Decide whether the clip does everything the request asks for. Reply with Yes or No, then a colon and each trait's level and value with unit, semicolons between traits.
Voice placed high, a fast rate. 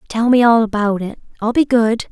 Yes: high, 230 Hz; fast, 225 wpm